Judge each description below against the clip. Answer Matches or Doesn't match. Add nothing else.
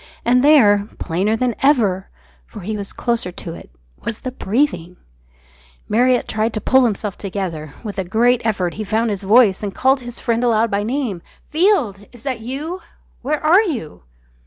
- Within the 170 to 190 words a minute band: Matches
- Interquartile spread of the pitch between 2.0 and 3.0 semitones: Doesn't match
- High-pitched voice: Matches